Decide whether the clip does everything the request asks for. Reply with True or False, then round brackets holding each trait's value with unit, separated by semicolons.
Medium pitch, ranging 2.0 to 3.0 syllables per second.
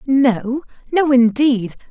False (255 Hz; 2.9 syllables/s)